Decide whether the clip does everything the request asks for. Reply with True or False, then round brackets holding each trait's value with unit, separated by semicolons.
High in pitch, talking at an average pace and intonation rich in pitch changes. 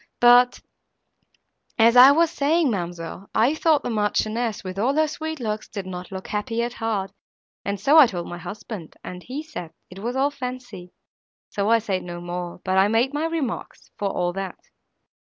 True (220 Hz; 185 wpm; 5.7 semitones)